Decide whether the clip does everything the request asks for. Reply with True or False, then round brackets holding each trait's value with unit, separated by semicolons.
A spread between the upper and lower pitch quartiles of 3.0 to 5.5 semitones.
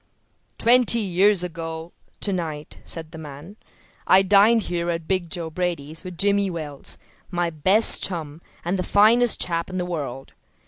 True (3.5 semitones)